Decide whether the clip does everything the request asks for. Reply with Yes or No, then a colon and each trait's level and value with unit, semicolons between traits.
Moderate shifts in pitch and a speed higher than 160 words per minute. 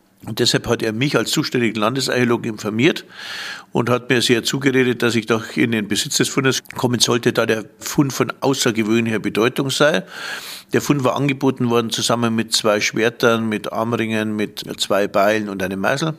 Yes: average, 3.1 semitones; average, 180 wpm